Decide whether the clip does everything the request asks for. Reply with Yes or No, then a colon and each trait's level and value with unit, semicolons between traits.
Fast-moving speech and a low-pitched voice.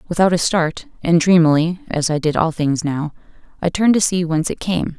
No: fast, 215 wpm; medium, 170 Hz